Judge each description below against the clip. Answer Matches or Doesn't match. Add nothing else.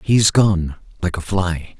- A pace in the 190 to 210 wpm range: Matches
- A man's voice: Matches